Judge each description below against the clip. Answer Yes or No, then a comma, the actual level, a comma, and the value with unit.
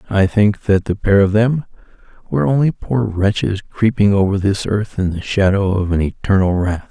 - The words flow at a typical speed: Yes, average, 190 wpm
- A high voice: No, low, 100 Hz